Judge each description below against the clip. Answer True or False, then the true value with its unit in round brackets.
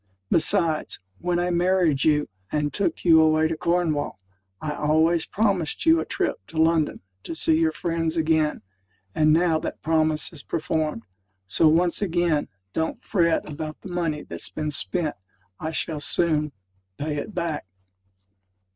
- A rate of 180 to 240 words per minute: False (150 wpm)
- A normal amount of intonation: False (2.1 semitones)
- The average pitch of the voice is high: False (160 Hz)